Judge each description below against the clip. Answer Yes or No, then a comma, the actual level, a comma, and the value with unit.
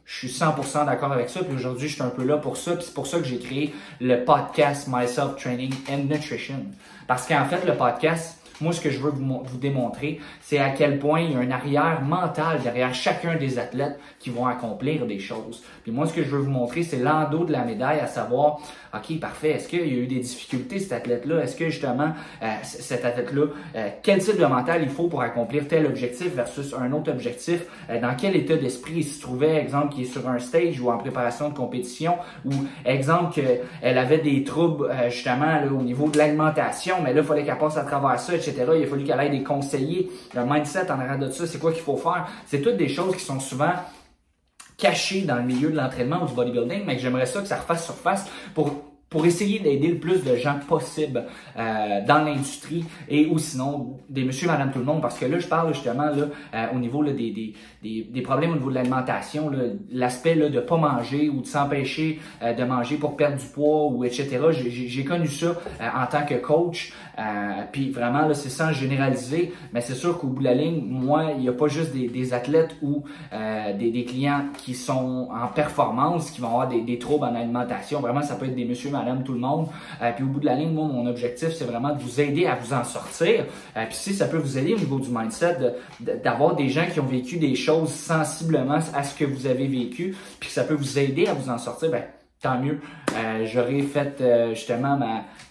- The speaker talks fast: Yes, fast, 235 wpm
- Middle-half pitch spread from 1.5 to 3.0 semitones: No, average, 3.8 semitones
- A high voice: No, medium, 140 Hz